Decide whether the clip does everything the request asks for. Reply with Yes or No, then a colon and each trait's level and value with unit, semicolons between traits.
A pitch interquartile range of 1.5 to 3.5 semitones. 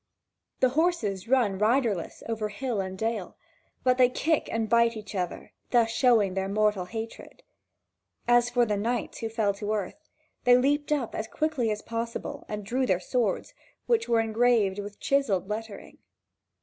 Yes: average, 3.2 semitones